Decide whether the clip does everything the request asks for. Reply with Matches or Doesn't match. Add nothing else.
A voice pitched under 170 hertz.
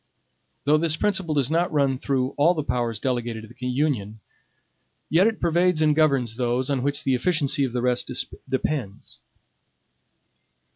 Matches